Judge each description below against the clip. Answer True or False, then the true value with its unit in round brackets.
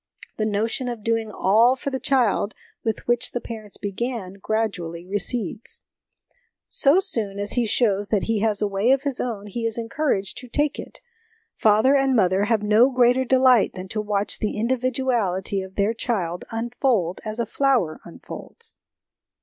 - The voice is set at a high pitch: True (225 Hz)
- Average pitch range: True (3.6 semitones)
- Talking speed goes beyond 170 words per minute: False (165 wpm)